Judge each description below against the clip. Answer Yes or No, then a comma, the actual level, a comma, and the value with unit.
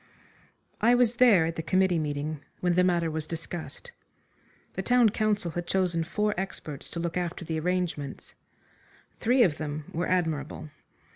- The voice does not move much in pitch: No, average, 3.3 semitones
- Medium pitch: Yes, medium, 175 Hz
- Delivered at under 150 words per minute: No, average, 155 wpm